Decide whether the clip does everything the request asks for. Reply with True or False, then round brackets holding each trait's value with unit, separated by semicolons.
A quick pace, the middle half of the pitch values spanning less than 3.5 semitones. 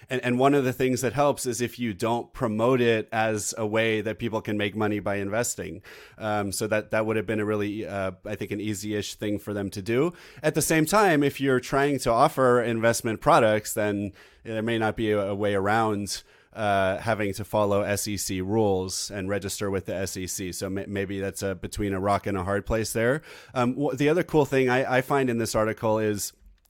True (220 wpm; 3.1 semitones)